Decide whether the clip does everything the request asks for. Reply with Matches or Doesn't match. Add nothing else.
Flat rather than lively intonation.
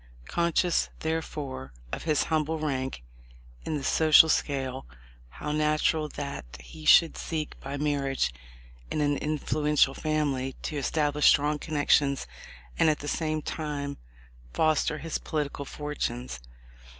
Matches